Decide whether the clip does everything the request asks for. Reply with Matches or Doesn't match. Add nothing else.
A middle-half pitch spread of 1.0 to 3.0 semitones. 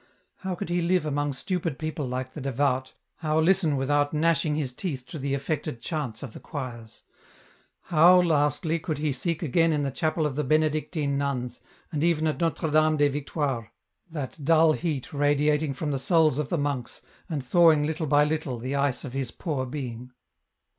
Matches